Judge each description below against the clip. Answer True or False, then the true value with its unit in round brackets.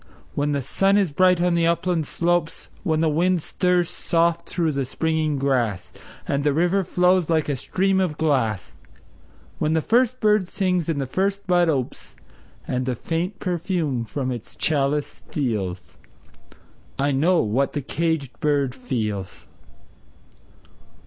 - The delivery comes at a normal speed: True (150 wpm)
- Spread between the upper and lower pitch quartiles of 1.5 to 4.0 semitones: False (4.5 semitones)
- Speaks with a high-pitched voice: False (160 Hz)